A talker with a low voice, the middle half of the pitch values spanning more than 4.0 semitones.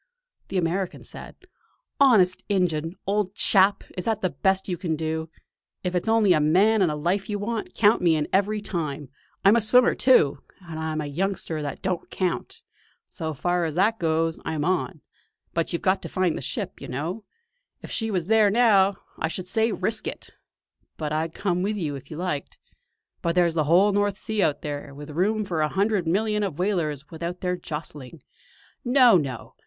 No: medium, 180 Hz; average, 4.4 semitones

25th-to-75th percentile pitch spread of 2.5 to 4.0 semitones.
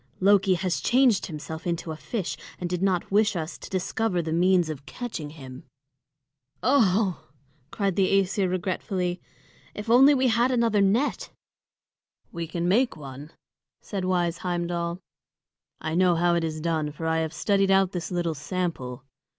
Yes: average, 3.3 semitones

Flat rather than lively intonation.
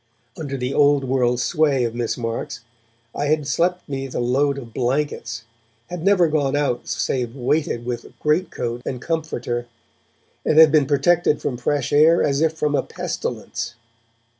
No: average, 3.9 semitones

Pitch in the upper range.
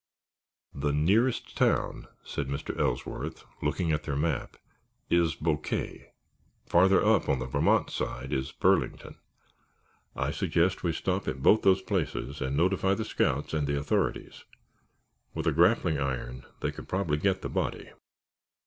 No: very low, 80 Hz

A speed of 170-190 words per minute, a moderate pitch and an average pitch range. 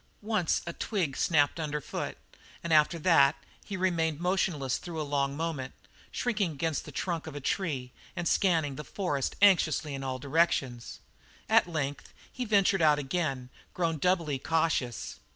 No: average, 155 wpm; medium, 160 Hz; average, 4.0 semitones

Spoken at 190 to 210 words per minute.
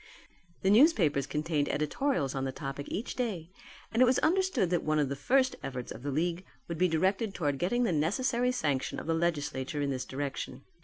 Yes: average, 200 wpm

